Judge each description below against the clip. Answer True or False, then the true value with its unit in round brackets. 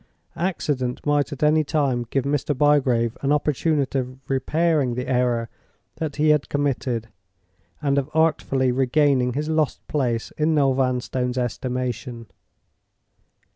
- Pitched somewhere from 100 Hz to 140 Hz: True (135 Hz)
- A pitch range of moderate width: True (3.0 semitones)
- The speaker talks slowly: True (130 wpm)